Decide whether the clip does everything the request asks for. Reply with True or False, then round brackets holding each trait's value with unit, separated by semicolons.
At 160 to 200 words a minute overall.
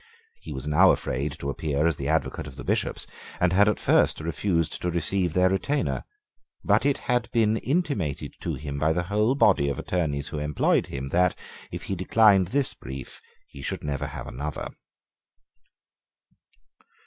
True (170 wpm)